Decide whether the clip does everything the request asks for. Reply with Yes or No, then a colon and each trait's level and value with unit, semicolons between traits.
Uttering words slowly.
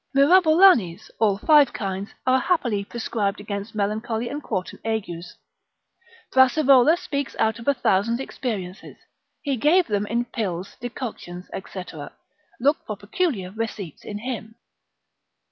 Yes: slow, 125 wpm